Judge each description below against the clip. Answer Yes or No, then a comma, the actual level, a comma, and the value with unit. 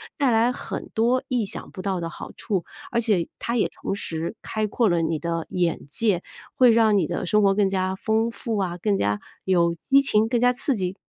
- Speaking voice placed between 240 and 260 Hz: No, high, 205 Hz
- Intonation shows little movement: No, average, 4.6 semitones